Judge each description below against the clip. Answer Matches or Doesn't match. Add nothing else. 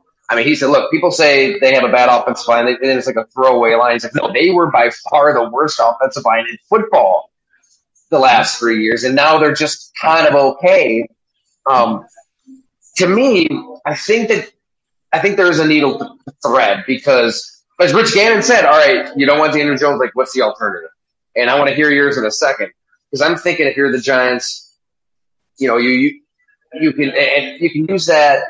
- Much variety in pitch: Matches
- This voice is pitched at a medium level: Matches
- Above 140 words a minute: Matches